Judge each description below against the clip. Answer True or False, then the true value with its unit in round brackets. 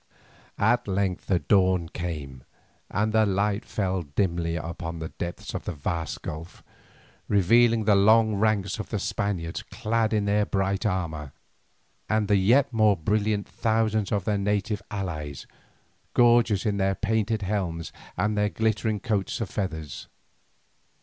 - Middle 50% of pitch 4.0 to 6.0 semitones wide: False (3.5 semitones)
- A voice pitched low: True (100 Hz)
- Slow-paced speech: False (145 wpm)